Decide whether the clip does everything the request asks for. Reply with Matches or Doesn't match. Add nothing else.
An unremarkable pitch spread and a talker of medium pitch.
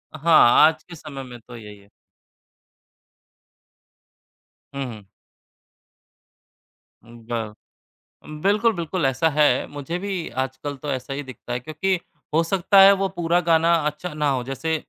Matches